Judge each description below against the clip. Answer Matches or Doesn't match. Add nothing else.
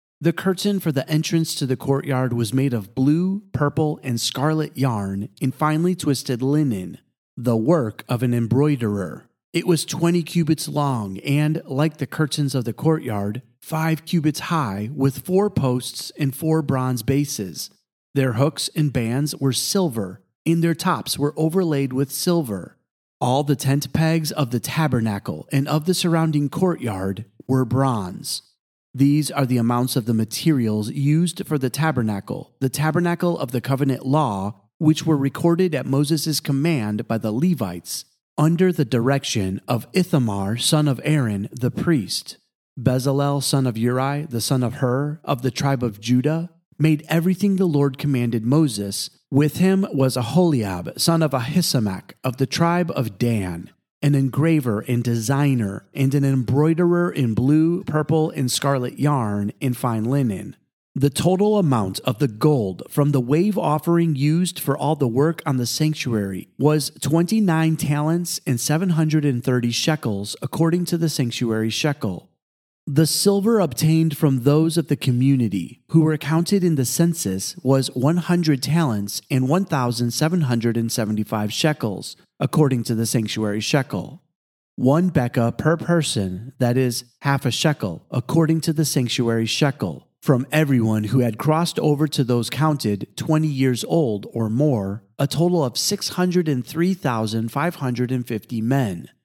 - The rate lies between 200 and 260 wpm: Doesn't match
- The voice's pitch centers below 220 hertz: Matches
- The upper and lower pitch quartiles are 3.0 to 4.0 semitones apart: Doesn't match